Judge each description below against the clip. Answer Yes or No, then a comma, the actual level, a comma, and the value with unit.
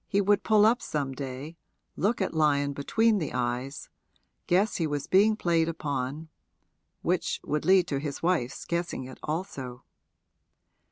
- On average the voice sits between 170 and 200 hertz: No, medium, 155 Hz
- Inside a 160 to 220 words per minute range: No, average, 150 wpm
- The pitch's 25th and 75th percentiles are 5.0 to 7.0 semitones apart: Yes, average, 5.3 semitones